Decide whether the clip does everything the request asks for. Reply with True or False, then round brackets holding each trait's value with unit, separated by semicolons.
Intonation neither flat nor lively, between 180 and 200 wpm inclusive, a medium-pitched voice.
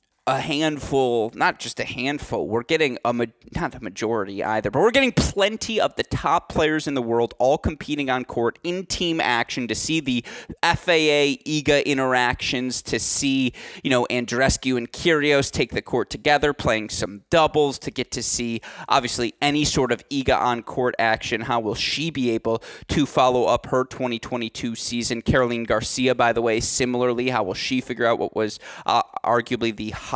False (3.5 semitones; 185 wpm; 125 Hz)